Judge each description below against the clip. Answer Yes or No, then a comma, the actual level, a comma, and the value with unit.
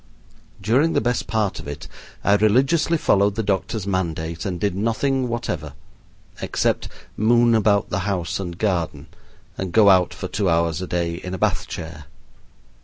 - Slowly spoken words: No, average, 165 wpm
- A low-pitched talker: Yes, low, 100 Hz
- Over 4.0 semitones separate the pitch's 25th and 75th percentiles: Yes, average, 4.4 semitones